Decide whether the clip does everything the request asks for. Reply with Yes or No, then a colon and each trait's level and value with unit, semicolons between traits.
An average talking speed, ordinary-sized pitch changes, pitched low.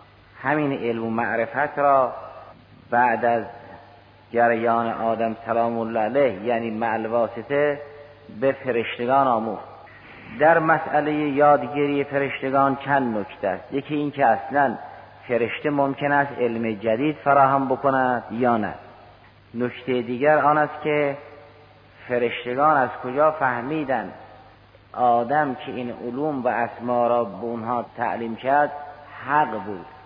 Yes: average, 120 wpm; average, 3.7 semitones; low, 125 Hz